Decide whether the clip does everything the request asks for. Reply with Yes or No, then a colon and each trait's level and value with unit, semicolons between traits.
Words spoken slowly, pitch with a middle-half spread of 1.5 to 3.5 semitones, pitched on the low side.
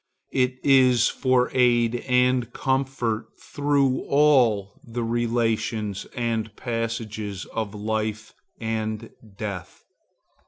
Yes: slow, 90 wpm; narrow, 2.5 semitones; low, 115 Hz